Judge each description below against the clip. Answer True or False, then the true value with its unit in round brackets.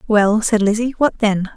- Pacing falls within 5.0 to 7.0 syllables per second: False (4.4 syllables/s)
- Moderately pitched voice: False (215 Hz)